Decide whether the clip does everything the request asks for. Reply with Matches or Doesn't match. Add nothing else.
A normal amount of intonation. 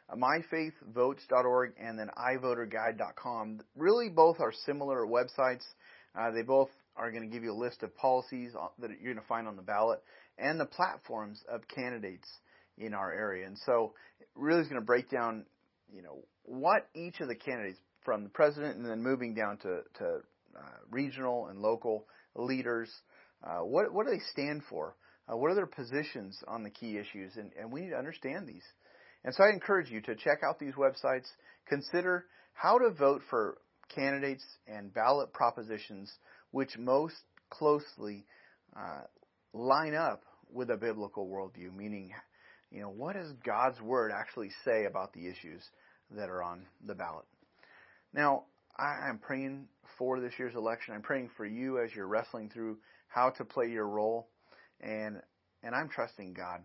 Matches